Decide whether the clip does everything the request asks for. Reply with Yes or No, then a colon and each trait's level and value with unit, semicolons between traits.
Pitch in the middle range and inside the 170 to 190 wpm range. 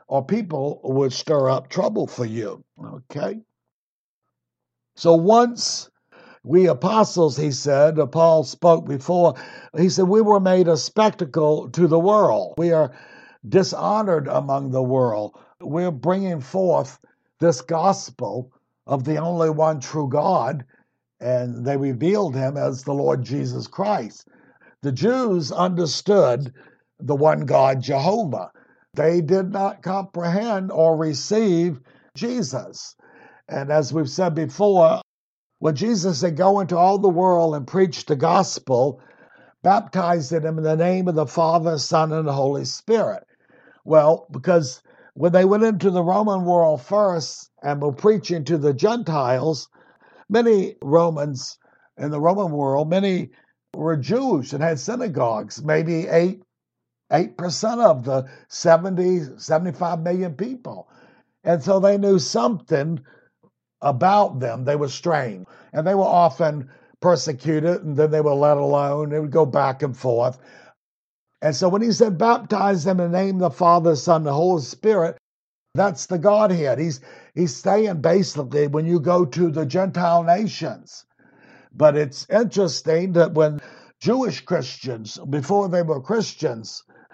No: medium, 165 Hz; average, 140 wpm